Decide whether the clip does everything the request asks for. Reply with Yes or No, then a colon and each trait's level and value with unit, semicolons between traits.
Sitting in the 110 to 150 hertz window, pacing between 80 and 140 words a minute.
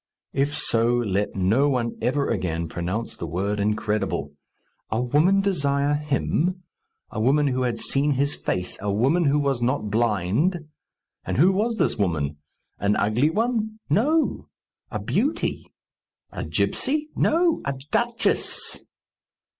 Yes: low, 135 Hz; slow, 135 wpm